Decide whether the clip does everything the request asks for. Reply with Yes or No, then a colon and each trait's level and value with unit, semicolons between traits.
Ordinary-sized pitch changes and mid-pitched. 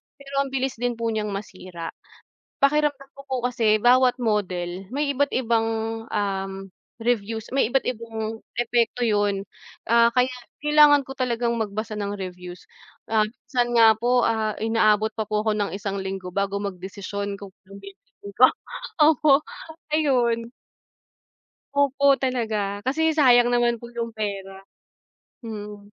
No: average, 3.7 semitones; high, 225 Hz